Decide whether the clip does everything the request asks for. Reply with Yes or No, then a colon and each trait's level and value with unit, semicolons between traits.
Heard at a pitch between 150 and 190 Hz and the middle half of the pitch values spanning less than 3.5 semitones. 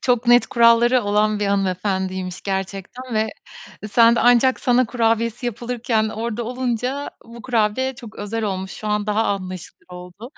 No: high, 225 Hz; average, 3.1 semitones